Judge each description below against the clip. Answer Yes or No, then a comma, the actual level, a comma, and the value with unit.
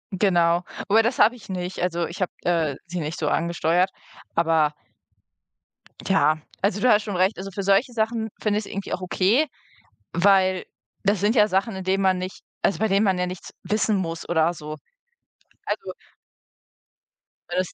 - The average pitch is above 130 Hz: Yes, medium, 185 Hz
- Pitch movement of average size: Yes, average, 3.0 semitones